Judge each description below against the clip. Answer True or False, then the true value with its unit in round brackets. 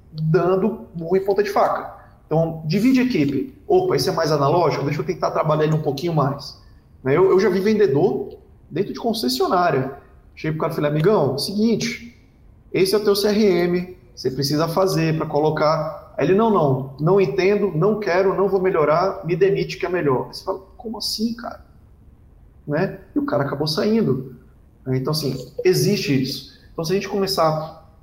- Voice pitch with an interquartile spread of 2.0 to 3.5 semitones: False (5.3 semitones)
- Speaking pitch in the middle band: True (180 Hz)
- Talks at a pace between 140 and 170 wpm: False (180 wpm)